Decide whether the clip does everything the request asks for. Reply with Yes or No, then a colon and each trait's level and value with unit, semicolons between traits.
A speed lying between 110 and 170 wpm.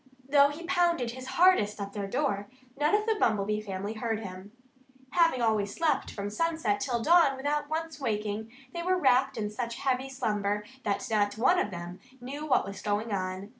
No: average, 185 wpm